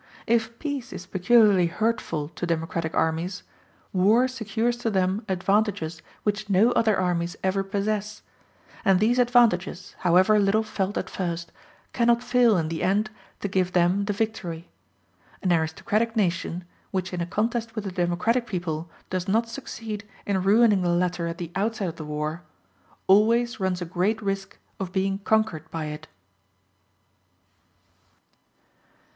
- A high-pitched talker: Yes, high, 195 Hz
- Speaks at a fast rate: No, average, 145 wpm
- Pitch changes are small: No, average, 3.8 semitones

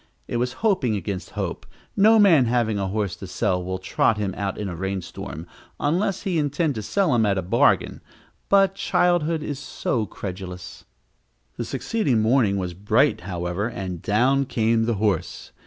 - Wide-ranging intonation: Yes, wide, 7.1 semitones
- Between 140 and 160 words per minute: No, average, 170 wpm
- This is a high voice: No, low, 110 Hz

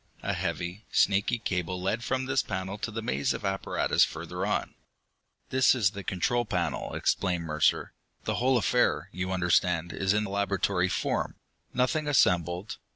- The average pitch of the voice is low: Yes, very low, 95 Hz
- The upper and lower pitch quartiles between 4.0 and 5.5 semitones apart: Yes, average, 4.6 semitones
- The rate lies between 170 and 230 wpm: No, average, 155 wpm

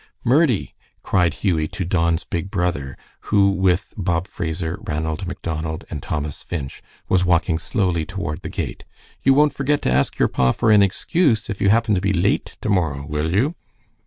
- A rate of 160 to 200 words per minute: Yes, average, 180 wpm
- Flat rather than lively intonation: No, average, 4.2 semitones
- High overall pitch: No, very low, 90 Hz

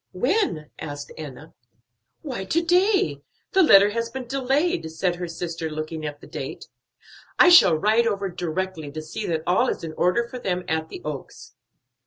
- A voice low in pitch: No, medium, 180 Hz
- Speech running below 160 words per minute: No, average, 175 wpm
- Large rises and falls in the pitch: Yes, wide, 7.6 semitones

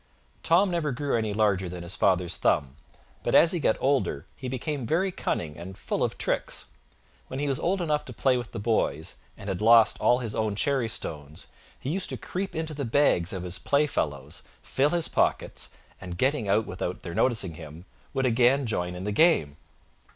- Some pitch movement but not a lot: No, wide, 7.8 semitones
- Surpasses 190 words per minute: Yes, average, 200 wpm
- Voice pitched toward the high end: No, low, 115 Hz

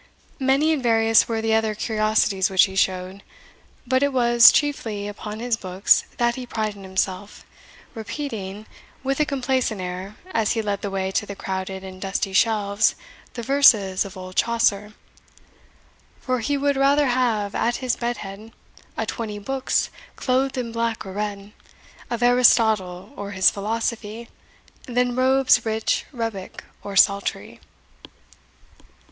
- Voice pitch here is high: Yes, high, 220 Hz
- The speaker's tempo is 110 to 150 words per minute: Yes, average, 145 wpm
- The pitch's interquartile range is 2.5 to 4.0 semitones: Yes, average, 3.7 semitones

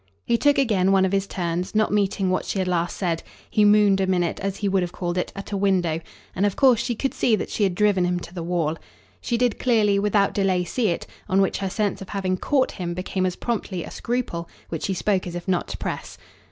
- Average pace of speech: No, fast, 250 wpm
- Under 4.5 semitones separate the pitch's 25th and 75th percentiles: Yes, average, 2.7 semitones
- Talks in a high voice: Yes, high, 195 Hz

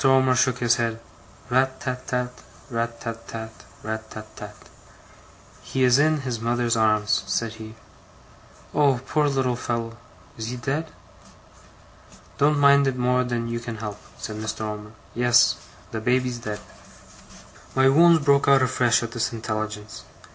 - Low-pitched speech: Yes, low, 120 Hz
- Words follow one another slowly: No, average, 150 wpm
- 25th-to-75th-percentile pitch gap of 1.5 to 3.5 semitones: Yes, average, 2.9 semitones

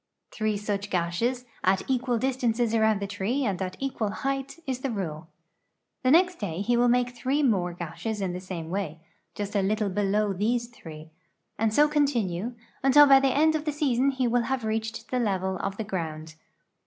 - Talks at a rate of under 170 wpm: No, average, 190 wpm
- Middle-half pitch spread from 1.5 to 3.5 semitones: No, average, 5.0 semitones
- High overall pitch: Yes, high, 220 Hz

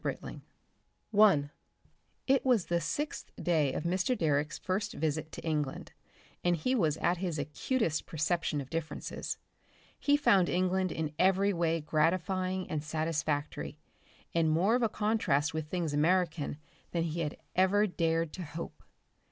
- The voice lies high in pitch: No, medium, 170 Hz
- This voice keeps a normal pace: Yes, average, 150 wpm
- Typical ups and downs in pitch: Yes, average, 3.4 semitones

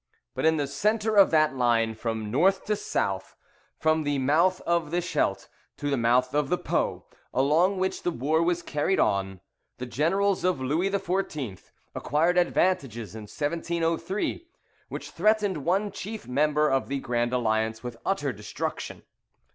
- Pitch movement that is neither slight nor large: No, wide, 6.5 semitones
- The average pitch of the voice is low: No, medium, 150 Hz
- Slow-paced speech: No, average, 155 wpm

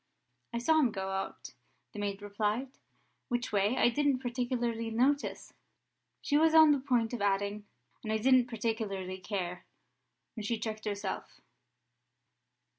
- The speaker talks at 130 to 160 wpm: Yes, average, 145 wpm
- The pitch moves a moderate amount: Yes, average, 3.7 semitones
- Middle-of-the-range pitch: No, high, 225 Hz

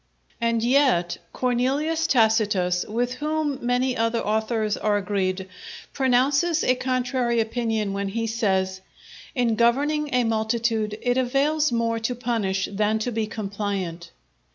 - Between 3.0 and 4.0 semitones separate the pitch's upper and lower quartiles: Yes, average, 3.3 semitones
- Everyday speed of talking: No, slow, 130 wpm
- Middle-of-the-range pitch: No, high, 230 Hz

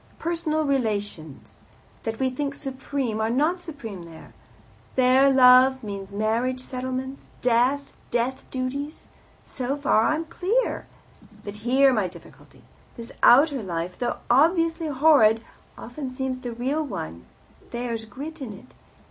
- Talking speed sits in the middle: No, slow, 130 wpm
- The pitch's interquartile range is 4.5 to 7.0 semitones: No, average, 4.1 semitones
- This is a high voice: Yes, very high, 255 Hz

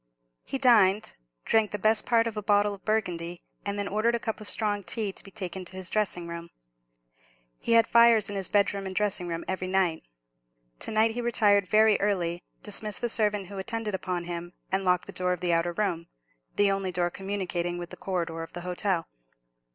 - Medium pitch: No, high, 195 Hz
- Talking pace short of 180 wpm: No, fast, 205 wpm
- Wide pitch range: No, average, 3.1 semitones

